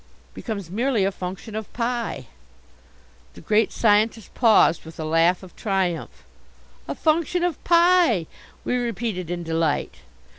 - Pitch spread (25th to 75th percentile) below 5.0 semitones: No, wide, 5.4 semitones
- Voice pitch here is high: Yes, high, 210 Hz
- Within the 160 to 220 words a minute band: No, slow, 135 wpm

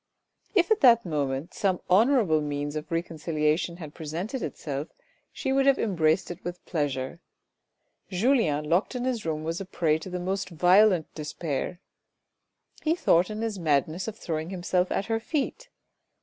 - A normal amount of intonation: No, wide, 5.7 semitones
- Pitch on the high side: No, medium, 175 Hz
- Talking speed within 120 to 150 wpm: No, average, 165 wpm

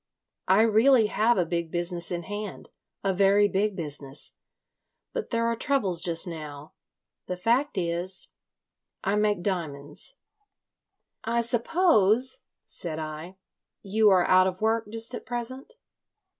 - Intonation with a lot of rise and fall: No, average, 4.9 semitones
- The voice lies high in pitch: Yes, high, 200 Hz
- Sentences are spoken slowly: Yes, slow, 130 wpm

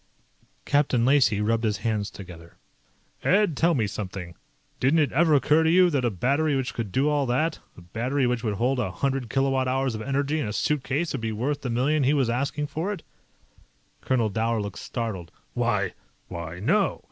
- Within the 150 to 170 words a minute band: No, average, 195 wpm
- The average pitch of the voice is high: No, low, 130 Hz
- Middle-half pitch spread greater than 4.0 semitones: Yes, average, 4.8 semitones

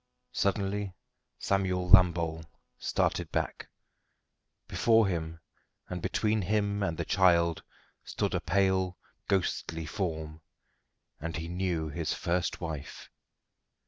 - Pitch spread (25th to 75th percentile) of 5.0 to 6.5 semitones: No, average, 3.0 semitones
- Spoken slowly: Yes, slow, 105 wpm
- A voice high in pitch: No, very low, 90 Hz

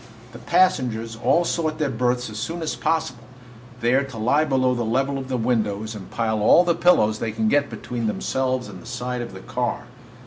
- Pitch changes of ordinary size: Yes, average, 3.9 semitones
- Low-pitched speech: Yes, low, 125 Hz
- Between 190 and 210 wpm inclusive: Yes, fast, 205 wpm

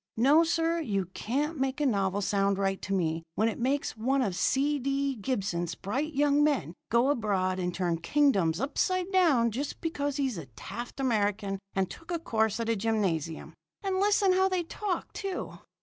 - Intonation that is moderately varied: No, wide, 7.1 semitones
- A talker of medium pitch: No, high, 245 Hz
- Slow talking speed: No, average, 180 wpm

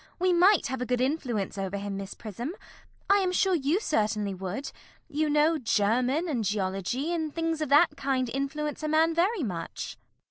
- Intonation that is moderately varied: No, wide, 7.3 semitones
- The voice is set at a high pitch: Yes, very high, 275 Hz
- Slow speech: No, average, 180 wpm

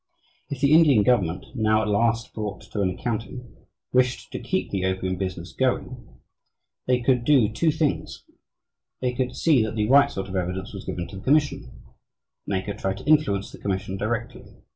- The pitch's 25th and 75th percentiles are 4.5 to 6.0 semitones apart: Yes, average, 4.8 semitones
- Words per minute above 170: Yes, average, 185 wpm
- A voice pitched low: Yes, low, 110 Hz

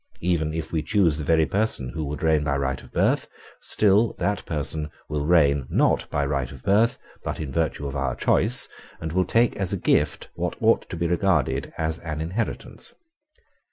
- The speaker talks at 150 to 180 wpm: No, average, 190 wpm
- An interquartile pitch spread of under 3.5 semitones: No, average, 4.0 semitones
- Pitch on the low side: Yes, very low, 80 Hz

